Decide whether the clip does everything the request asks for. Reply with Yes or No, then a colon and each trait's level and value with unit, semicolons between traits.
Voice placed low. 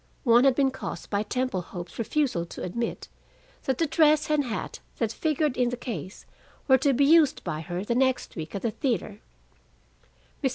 No: high, 245 Hz